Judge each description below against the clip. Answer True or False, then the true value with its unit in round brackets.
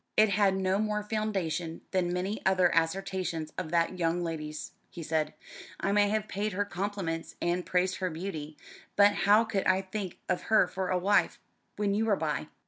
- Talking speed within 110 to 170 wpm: False (185 wpm)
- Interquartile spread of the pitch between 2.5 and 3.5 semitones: True (3.2 semitones)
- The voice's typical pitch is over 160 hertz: True (185 Hz)